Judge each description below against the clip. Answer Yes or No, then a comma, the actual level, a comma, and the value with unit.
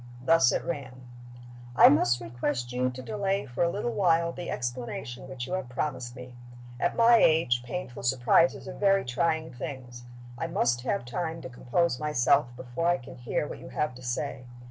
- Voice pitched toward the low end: Yes, low, 130 Hz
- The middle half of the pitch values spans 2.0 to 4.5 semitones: No, wide, 5.4 semitones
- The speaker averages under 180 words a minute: No, average, 185 wpm